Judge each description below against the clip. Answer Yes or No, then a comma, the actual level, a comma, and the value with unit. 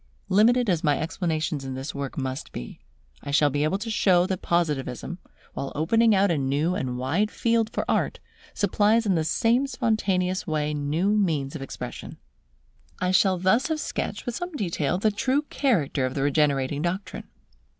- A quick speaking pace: No, average, 175 wpm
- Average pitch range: No, wide, 6.5 semitones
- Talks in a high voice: No, medium, 175 Hz